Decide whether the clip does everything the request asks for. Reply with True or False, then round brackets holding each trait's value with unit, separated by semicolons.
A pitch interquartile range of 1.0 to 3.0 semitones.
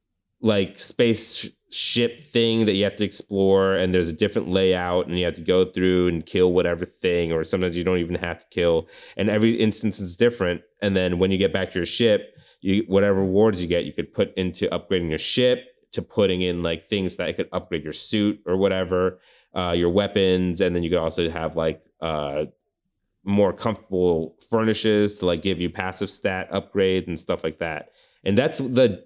True (2.5 semitones)